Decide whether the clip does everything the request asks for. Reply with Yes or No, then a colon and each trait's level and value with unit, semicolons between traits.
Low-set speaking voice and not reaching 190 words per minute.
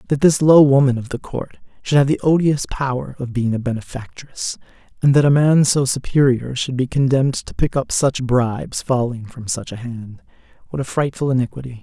No: low, 130 Hz; average, 200 wpm